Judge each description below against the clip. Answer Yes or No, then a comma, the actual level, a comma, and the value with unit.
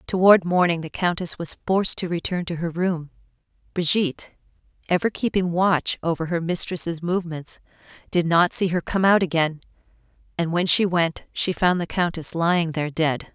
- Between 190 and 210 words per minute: No, average, 165 wpm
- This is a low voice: No, medium, 170 Hz